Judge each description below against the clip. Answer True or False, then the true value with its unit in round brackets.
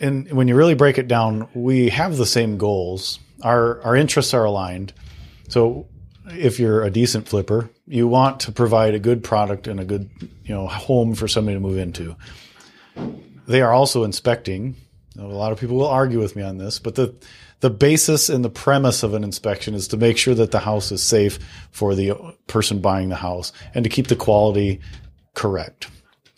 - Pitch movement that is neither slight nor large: True (4.0 semitones)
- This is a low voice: True (110 Hz)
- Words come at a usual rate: True (195 wpm)